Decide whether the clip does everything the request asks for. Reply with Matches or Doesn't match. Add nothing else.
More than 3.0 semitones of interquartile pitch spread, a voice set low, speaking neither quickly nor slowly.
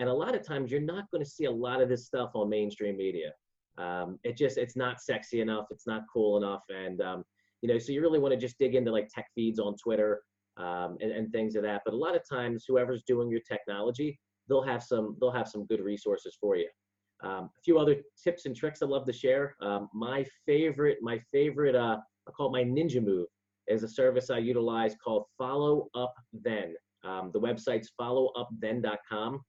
Doesn't match